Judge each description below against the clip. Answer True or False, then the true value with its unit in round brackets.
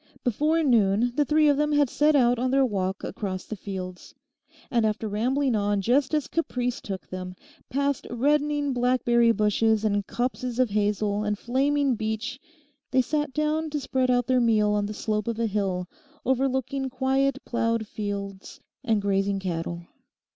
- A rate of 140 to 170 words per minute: True (165 wpm)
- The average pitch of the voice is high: True (235 Hz)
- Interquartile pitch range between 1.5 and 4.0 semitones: False (4.6 semitones)